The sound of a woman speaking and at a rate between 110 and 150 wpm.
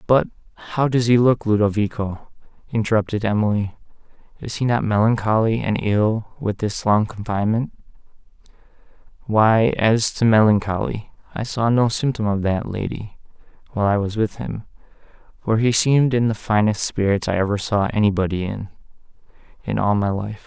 No: male; average, 145 wpm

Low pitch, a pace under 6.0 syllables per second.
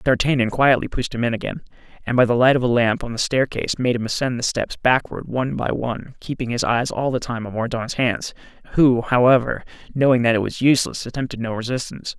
No: low, 125 Hz; 6.1 syllables/s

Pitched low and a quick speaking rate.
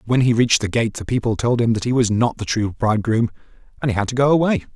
Yes: low, 115 Hz; fast, 290 wpm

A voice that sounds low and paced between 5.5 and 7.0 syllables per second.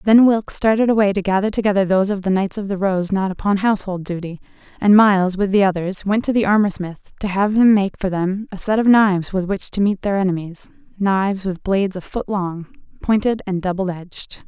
No: high, 195 Hz; 5.7 syllables/s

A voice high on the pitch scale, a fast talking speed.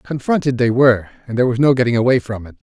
No: low, 125 Hz; fast, 245 wpm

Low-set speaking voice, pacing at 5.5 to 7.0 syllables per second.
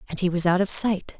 No: medium, 185 Hz; 6.1 syllables/s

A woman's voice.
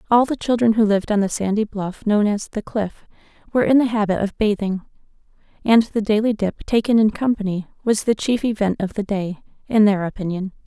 Yes: female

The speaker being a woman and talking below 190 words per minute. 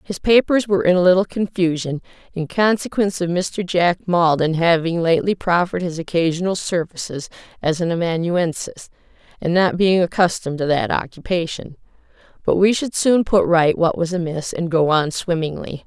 Yes: female; average, 160 wpm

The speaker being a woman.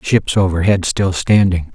No: male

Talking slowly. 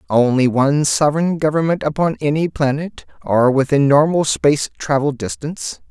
Yes: slow, 130 wpm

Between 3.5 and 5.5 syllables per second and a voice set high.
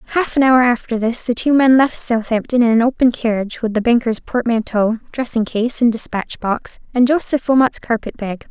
Yes: 5.3 syllables/s; high, 235 Hz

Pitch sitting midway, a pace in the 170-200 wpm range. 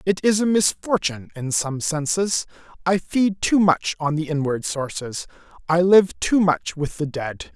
Yes: medium, 170 Hz; average, 175 wpm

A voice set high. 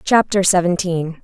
No: medium, 180 Hz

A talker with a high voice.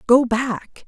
Yes: high, 240 Hz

